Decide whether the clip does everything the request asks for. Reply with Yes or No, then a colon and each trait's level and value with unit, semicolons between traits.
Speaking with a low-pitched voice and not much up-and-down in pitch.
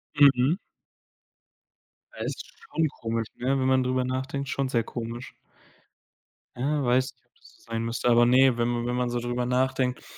Yes: low, 125 Hz; narrow, 1.7 semitones